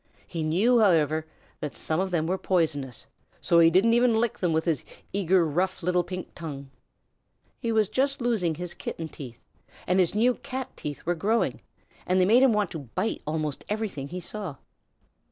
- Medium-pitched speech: Yes, medium, 180 Hz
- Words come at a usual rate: Yes, average, 190 wpm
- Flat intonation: No, average, 5.1 semitones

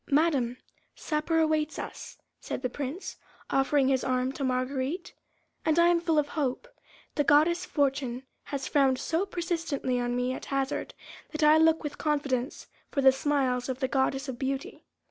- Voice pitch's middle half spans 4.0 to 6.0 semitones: No, average, 3.2 semitones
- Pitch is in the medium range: No, very high, 280 Hz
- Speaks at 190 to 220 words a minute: No, average, 165 wpm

